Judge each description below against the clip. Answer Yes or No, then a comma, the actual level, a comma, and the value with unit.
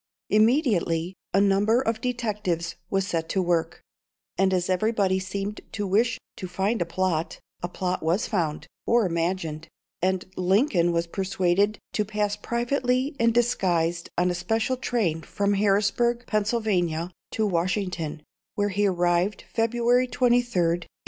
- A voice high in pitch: Yes, high, 195 Hz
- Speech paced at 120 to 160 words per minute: Yes, average, 140 wpm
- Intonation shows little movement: No, average, 4.2 semitones